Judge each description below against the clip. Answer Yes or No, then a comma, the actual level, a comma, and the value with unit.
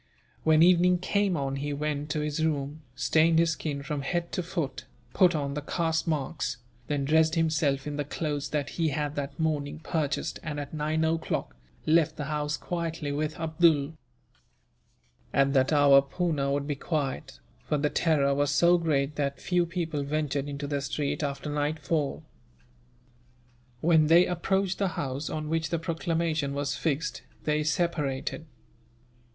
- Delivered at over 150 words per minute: Yes, average, 160 wpm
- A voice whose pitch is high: No, medium, 150 Hz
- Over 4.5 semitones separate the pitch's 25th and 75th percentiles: No, narrow, 2.4 semitones